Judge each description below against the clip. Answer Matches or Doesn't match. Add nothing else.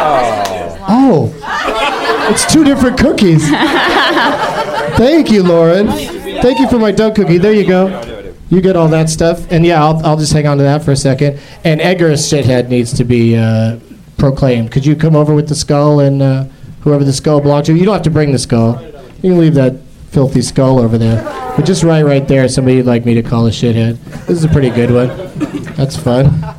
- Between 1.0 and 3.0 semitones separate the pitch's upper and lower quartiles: Doesn't match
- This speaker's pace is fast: Matches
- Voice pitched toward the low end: Doesn't match